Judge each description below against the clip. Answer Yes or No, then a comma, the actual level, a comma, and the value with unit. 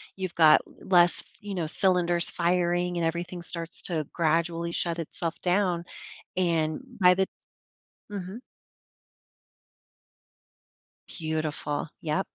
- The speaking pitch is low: No, medium, 175 Hz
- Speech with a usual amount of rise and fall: No, narrow, 1.7 semitones